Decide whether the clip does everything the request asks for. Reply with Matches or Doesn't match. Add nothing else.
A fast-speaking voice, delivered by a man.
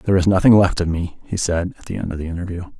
Matches